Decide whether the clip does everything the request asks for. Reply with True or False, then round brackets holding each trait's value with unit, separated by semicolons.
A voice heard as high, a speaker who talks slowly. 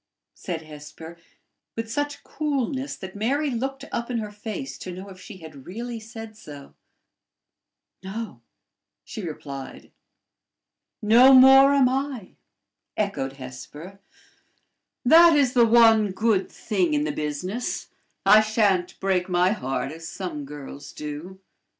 True (205 Hz; 130 wpm)